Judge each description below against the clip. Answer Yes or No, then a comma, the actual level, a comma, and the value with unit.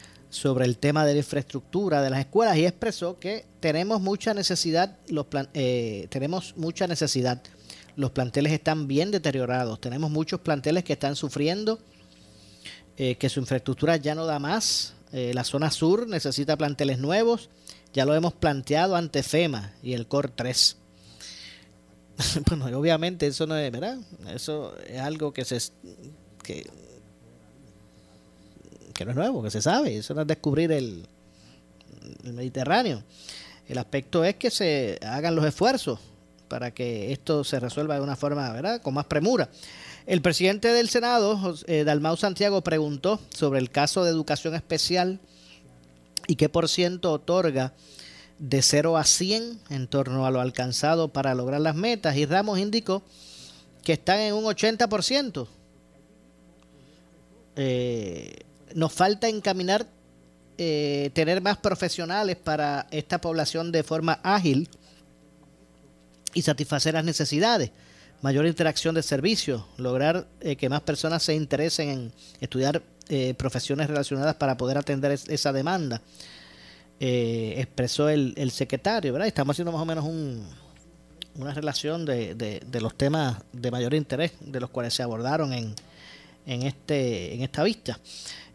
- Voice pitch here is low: No, medium, 145 Hz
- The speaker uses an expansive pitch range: No, average, 4.8 semitones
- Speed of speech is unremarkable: Yes, average, 145 wpm